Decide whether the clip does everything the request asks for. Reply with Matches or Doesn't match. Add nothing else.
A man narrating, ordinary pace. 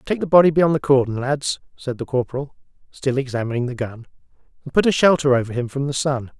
Doesn't match